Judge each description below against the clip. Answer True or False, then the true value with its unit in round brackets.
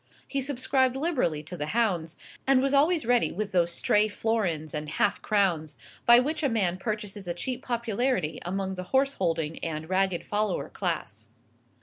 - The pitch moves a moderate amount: False (6.6 semitones)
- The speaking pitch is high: True (205 Hz)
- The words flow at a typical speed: True (165 wpm)